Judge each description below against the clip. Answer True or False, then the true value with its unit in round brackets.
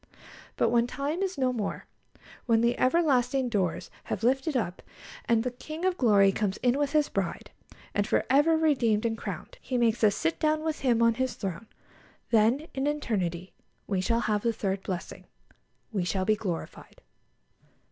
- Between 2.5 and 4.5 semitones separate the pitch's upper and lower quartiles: False (5.1 semitones)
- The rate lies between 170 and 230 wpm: True (180 wpm)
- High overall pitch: True (235 Hz)